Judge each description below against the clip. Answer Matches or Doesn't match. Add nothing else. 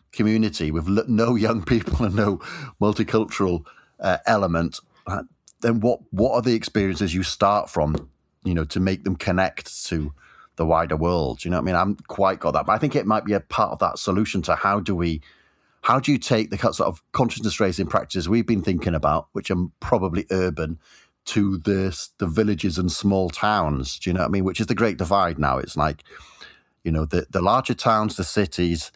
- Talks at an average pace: Doesn't match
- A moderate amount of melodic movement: Matches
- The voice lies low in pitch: Matches